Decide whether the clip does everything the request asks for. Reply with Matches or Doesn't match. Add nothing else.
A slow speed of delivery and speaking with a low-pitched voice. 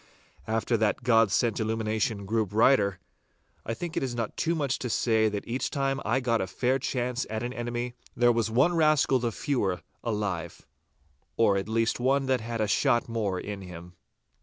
Doesn't match